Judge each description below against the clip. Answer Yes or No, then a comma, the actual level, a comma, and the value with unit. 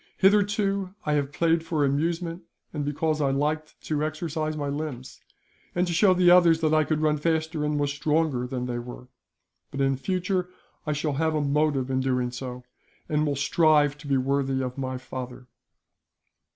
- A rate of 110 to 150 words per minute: No, average, 180 wpm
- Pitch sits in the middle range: Yes, medium, 150 Hz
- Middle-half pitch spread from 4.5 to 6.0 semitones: No, average, 3.1 semitones